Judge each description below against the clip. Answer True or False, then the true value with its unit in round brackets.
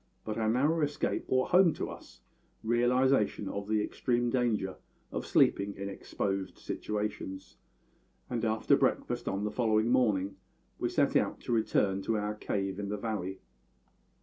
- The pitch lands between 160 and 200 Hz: False (105 Hz)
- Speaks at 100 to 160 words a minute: True (150 wpm)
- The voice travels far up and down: False (3.5 semitones)